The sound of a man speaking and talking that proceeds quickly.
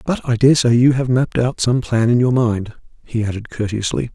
Yes: male; fast, 215 wpm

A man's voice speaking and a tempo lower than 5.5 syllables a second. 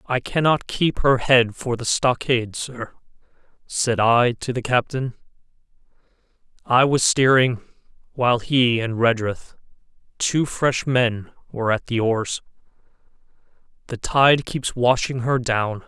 Yes: male; 4.0 syllables/s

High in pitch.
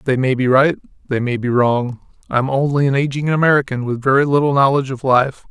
No: low, 135 Hz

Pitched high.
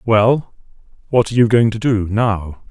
No: low, 110 Hz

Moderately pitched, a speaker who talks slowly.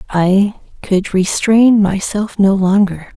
No: high, 200 Hz; slow, 115 wpm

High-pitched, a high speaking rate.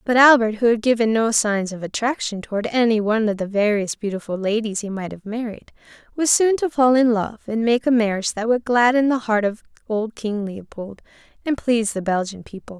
Yes: high, 220 Hz; fast, 210 wpm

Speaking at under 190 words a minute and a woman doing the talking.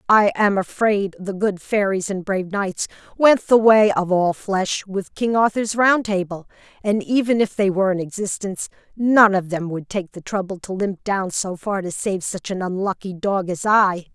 No: average, 200 wpm; female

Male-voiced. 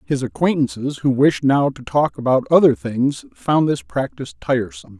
Yes: male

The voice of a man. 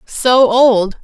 No: female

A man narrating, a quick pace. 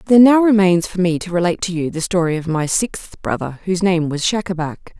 No: female; fast, 230 wpm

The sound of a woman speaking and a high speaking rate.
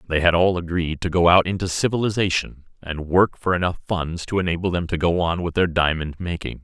No: male; fast, 215 wpm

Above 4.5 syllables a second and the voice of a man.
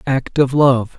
No: 3.5 syllables/s; male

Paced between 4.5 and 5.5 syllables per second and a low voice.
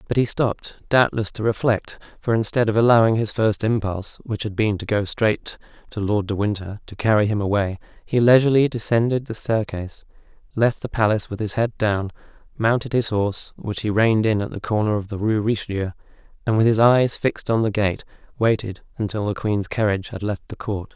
No: 5.7 syllables/s; low, 110 Hz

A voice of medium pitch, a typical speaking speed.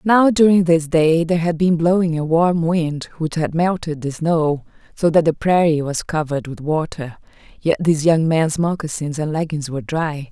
Yes: medium, 160 Hz; average, 190 wpm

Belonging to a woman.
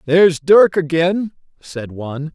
No: male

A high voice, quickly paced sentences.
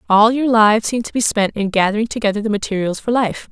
Yes: high, 215 Hz; fast, 240 wpm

